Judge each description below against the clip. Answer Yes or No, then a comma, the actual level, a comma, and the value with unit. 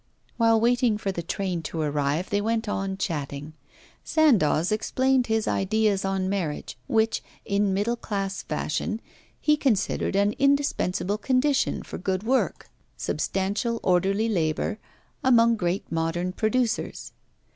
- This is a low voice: No, high, 205 Hz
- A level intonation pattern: No, average, 3.9 semitones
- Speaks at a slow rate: Yes, slow, 125 wpm